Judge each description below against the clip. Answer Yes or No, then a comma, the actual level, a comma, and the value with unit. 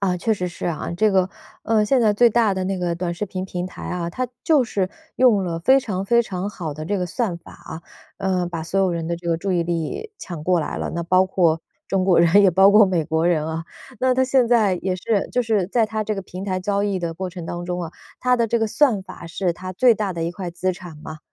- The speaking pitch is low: No, medium, 185 Hz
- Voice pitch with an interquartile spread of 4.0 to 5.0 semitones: No, average, 3.6 semitones